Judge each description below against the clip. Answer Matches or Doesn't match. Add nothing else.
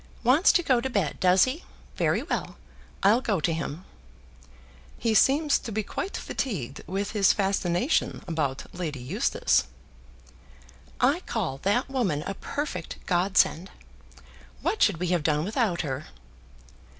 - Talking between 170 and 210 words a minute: Doesn't match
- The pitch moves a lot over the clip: Matches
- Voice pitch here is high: Matches